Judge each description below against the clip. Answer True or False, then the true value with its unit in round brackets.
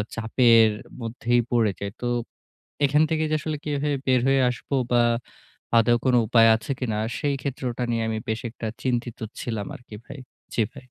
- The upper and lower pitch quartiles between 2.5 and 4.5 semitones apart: True (2.9 semitones)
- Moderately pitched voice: False (120 Hz)